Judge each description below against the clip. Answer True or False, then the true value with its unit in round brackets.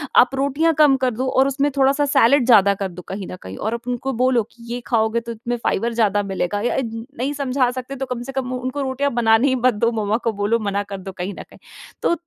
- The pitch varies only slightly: False (3.5 semitones)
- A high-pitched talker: True (245 Hz)